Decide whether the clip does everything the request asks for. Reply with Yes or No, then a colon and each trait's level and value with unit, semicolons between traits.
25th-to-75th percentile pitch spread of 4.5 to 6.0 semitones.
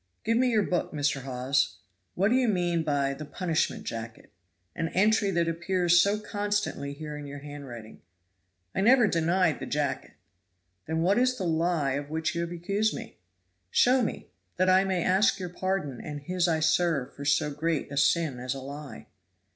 Yes: average, 4.9 semitones